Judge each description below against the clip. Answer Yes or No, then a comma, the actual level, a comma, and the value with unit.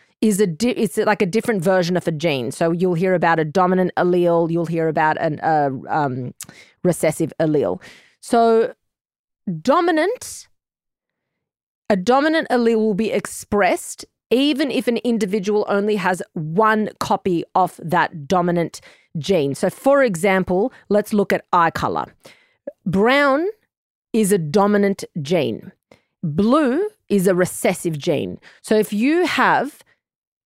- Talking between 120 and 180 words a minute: Yes, slow, 135 wpm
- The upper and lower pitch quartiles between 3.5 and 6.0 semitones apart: Yes, average, 4.9 semitones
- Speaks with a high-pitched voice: Yes, high, 200 Hz